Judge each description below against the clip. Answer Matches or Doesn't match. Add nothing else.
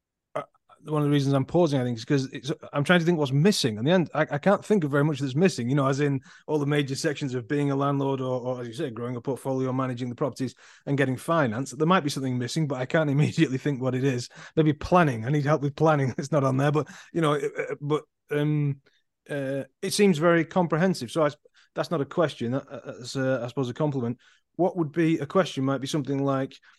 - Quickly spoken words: Matches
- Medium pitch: Matches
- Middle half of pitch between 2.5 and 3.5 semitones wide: Matches